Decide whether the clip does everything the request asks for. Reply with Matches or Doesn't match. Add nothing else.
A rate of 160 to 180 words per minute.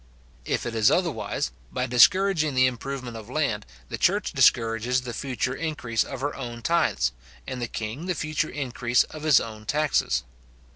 Matches